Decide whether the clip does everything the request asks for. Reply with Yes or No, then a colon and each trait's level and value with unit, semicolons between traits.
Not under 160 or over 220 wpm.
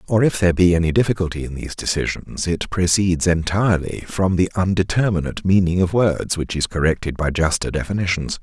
Yes: average, 170 wpm